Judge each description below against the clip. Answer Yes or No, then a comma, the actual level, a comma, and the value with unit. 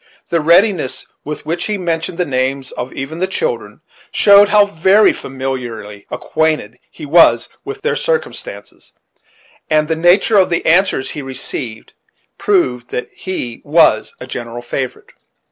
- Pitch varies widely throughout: Yes, wide, 6.5 semitones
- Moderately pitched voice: Yes, medium, 160 Hz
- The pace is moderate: Yes, average, 145 wpm